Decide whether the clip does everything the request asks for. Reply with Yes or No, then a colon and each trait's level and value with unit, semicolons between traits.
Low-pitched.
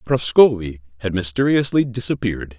Yes: low, 110 Hz